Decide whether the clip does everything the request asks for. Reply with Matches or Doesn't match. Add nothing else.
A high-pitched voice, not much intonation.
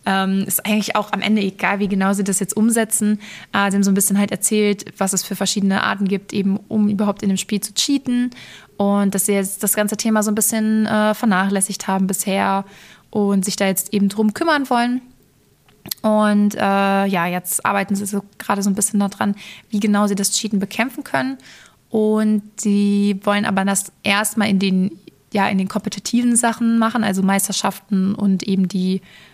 Matches